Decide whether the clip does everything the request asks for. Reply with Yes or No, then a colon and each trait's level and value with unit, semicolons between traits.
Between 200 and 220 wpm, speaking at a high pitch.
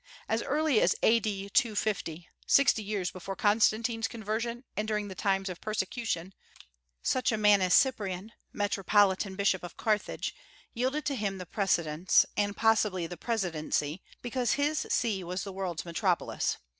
No: average, 145 wpm; high, 205 Hz